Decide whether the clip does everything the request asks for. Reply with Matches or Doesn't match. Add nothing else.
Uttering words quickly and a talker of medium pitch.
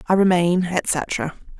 Doesn't match